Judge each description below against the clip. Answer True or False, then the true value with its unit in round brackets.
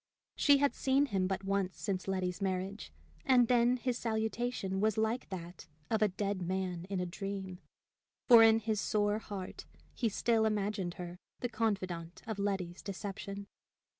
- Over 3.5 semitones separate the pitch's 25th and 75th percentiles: False (2.9 semitones)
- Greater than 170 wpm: False (160 wpm)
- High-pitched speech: True (200 Hz)